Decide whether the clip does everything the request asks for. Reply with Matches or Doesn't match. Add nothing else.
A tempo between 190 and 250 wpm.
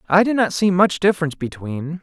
Matches